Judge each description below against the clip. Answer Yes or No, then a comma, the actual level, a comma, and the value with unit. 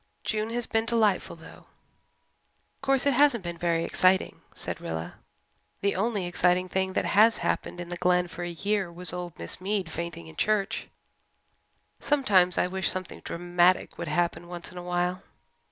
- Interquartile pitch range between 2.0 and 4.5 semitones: Yes, average, 3.1 semitones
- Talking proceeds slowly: No, average, 170 wpm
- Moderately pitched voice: Yes, medium, 180 Hz